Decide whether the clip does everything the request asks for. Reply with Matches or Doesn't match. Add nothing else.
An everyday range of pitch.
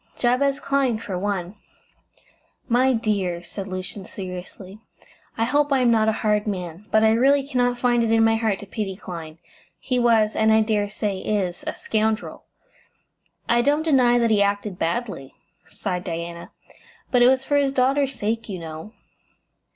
Matches